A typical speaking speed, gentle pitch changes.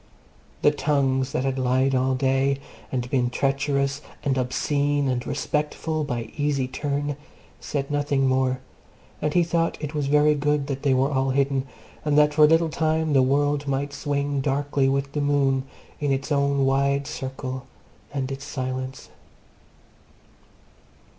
Yes: average, 155 wpm; narrow, 1.6 semitones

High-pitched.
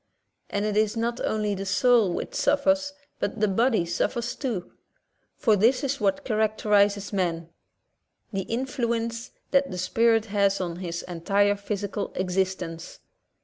Yes: high, 205 Hz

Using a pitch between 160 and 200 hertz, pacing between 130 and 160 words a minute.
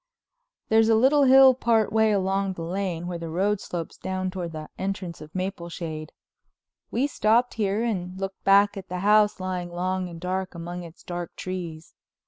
No: medium, 185 Hz; average, 175 wpm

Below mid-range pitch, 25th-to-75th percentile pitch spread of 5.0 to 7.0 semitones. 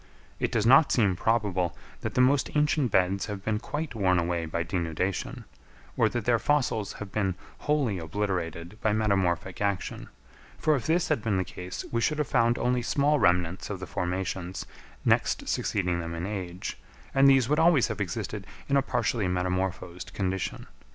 Yes: low, 100 Hz; average, 5.3 semitones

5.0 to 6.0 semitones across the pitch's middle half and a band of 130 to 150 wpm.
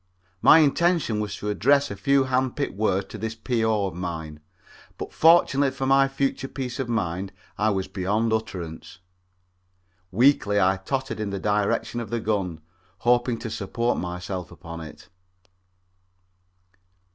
Yes: wide, 5.5 semitones; average, 145 wpm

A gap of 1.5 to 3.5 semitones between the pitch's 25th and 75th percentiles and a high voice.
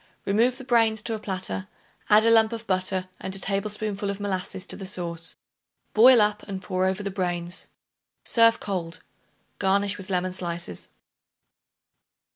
Yes: narrow, 2.6 semitones; high, 195 Hz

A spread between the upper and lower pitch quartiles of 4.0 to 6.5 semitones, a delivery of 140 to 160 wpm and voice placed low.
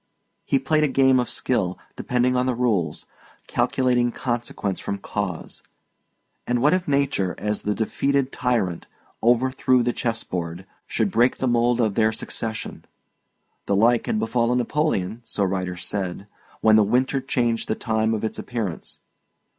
No: average, 3.6 semitones; average, 155 wpm; low, 115 Hz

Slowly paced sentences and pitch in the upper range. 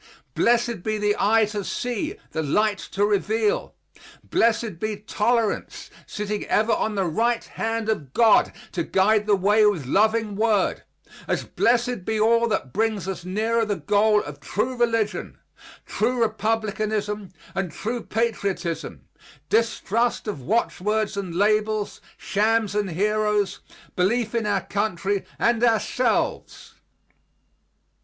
Yes: slow, 130 wpm; high, 215 Hz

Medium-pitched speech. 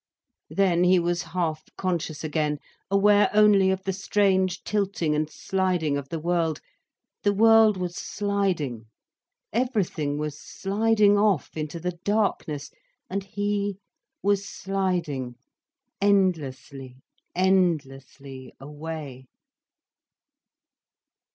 Yes: medium, 180 Hz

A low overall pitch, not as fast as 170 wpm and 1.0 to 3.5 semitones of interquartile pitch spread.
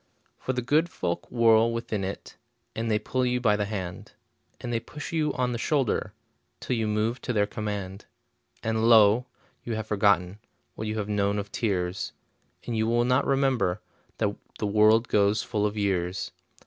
No: low, 110 Hz; average, 180 wpm; average, 2.7 semitones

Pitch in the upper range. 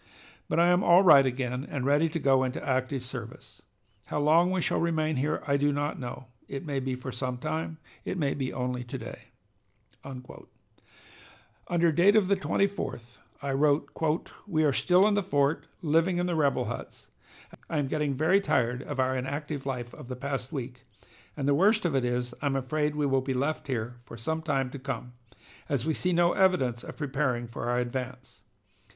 No: medium, 140 Hz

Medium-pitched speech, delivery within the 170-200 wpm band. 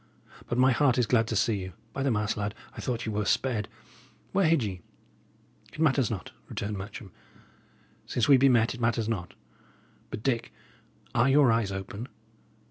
No: low, 115 Hz; average, 180 wpm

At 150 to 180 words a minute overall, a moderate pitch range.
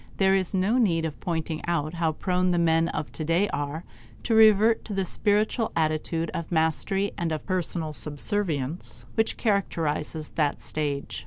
Yes: average, 160 wpm; average, 3.8 semitones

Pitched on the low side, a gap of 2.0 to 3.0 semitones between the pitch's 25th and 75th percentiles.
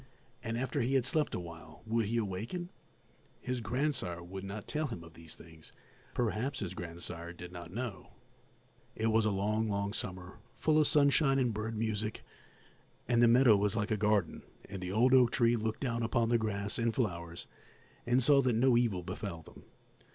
No: low, 110 Hz; average, 4.5 semitones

